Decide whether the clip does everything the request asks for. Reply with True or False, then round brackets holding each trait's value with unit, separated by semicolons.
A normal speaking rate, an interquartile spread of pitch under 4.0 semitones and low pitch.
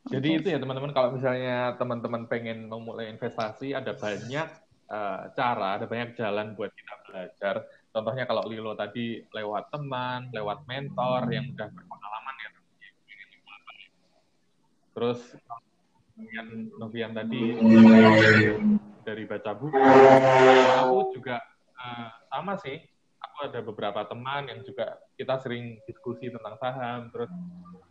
True (125 wpm; 2.7 semitones; 120 Hz)